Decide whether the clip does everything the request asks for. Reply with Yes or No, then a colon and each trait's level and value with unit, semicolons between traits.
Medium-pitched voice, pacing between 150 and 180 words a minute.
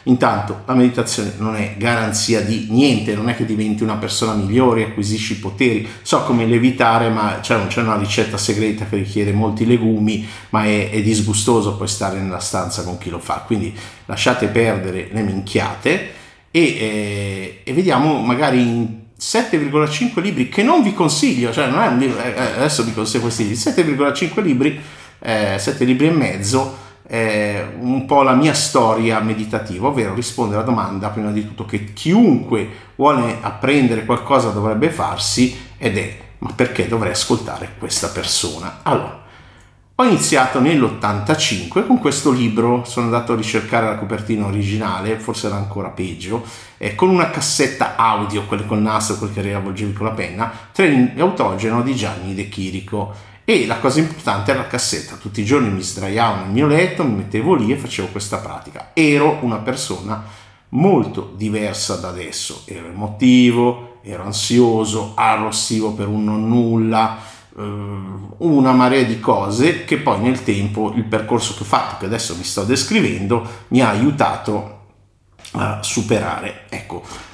No: low, 110 Hz; average, 155 wpm